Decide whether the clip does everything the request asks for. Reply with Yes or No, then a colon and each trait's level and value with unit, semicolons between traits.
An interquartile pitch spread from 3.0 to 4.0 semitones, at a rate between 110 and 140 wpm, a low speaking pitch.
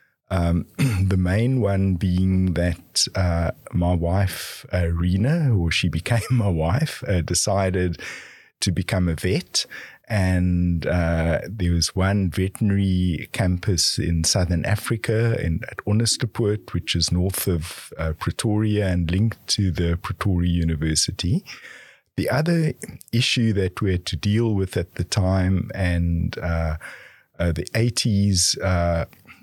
Yes: average, 3.5 semitones; slow, 135 wpm; very low, 95 Hz